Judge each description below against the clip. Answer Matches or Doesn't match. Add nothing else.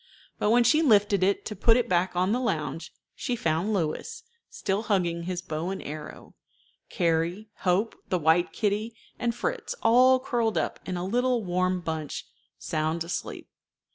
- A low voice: Doesn't match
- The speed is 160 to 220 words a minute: Matches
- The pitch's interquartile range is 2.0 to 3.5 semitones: Doesn't match